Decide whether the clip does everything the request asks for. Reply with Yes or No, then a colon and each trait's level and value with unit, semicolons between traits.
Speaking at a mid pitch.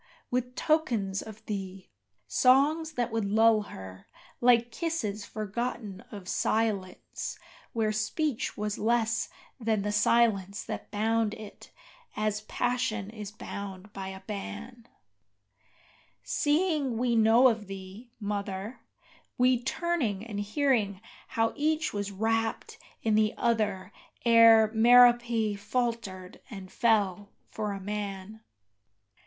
No: high, 220 Hz